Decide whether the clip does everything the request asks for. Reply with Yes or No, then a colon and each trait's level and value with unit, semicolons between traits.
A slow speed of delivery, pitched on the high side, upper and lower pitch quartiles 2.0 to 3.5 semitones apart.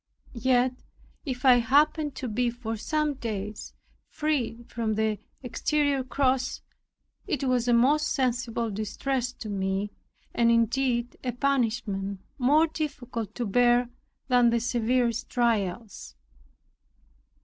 Yes: slow, 115 wpm; high, 245 Hz; average, 2.7 semitones